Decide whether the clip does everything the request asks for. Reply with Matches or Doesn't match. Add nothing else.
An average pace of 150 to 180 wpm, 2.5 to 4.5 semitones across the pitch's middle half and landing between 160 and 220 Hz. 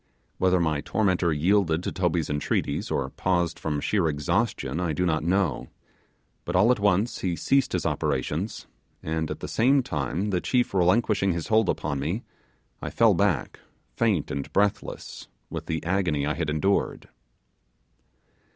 Doesn't match